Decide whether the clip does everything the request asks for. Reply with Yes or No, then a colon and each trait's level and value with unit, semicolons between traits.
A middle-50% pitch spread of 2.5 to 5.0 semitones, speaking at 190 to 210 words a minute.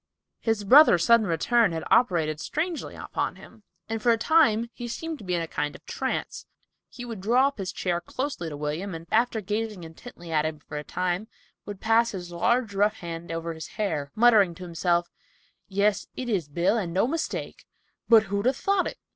No: wide, 5.4 semitones; average, 200 wpm